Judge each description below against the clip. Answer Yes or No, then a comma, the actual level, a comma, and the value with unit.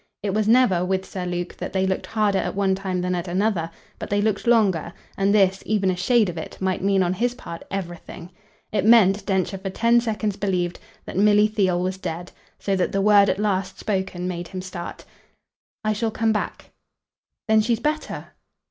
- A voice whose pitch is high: Yes, high, 195 Hz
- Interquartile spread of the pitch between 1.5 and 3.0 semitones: Yes, narrow, 2.6 semitones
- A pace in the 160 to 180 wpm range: No, average, 200 wpm